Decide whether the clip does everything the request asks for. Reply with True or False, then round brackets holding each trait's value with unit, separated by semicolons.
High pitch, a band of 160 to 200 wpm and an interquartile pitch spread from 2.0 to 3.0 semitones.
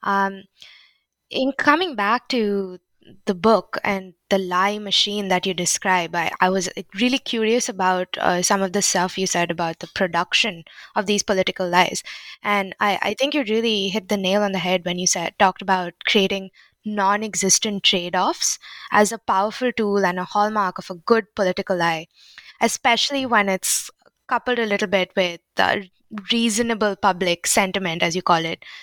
True (195 Hz; 170 wpm; 2.7 semitones)